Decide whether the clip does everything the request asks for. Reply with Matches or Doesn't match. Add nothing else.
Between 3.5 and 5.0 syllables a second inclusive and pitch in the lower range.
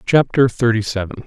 Doesn't match